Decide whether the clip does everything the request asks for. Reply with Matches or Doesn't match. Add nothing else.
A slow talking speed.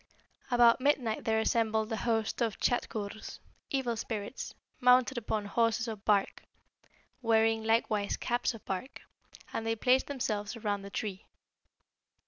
Matches